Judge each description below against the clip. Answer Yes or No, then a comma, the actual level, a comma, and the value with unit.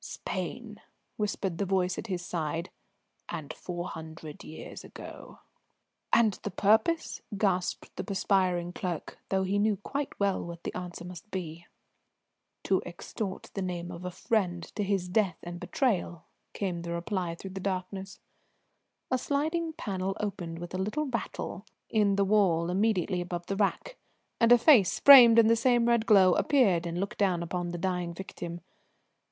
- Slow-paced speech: No, average, 160 wpm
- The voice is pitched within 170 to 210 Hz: Yes, high, 190 Hz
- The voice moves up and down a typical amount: Yes, average, 3.3 semitones